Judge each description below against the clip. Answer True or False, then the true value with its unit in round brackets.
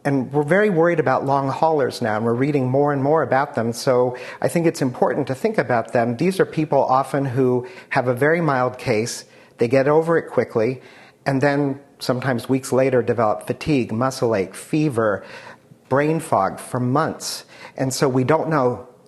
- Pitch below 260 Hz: True (135 Hz)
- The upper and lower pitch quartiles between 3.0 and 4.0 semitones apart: True (3.4 semitones)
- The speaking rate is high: False (185 wpm)